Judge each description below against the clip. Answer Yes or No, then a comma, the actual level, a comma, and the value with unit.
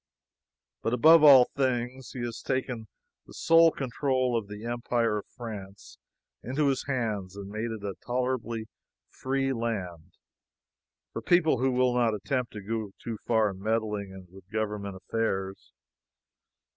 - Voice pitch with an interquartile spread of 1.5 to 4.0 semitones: Yes, average, 3.6 semitones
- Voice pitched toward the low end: Yes, low, 115 Hz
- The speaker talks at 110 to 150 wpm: Yes, average, 145 wpm